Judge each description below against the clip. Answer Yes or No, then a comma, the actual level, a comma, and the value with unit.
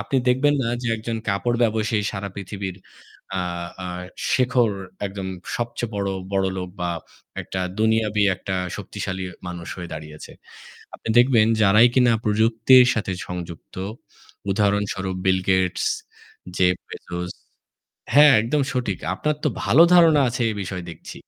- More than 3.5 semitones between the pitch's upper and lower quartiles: Yes, average, 4.2 semitones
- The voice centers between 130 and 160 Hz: No, low, 105 Hz